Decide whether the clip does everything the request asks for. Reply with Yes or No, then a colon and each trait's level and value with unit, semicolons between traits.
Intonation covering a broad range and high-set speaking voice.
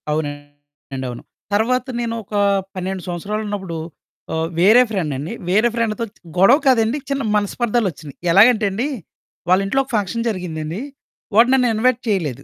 Yes: wide, 5.8 semitones; high, 205 Hz